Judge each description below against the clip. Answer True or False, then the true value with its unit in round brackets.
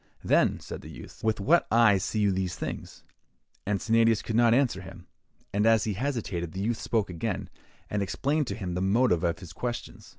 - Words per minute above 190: True (200 wpm)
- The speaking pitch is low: True (105 Hz)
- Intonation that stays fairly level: False (3.8 semitones)